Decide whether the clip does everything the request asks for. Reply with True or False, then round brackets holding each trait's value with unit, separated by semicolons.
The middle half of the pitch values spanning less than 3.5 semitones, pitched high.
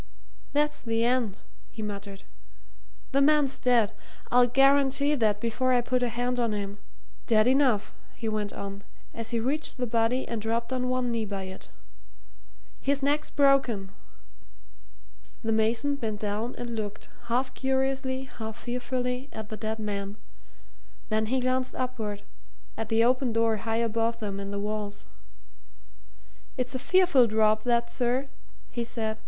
True (3.0 semitones; 235 Hz)